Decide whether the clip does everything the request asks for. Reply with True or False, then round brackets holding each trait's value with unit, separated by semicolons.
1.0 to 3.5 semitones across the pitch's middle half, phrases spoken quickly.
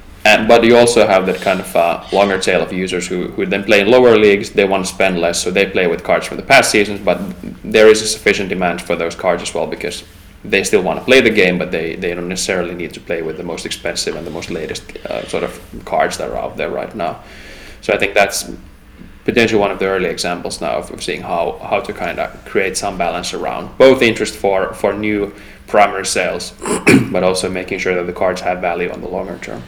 True (2.8 semitones; 245 wpm)